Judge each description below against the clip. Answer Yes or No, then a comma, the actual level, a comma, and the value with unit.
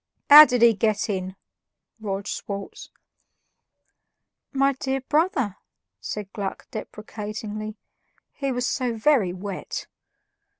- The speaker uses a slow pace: Yes, slow, 100 wpm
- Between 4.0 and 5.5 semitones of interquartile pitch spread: Yes, average, 4.7 semitones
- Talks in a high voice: Yes, high, 215 Hz